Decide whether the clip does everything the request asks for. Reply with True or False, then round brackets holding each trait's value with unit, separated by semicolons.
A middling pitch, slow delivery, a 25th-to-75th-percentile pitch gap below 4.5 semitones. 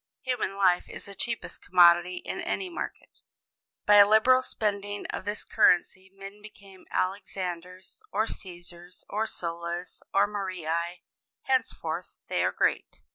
False (195 Hz; 130 wpm; 2.8 semitones)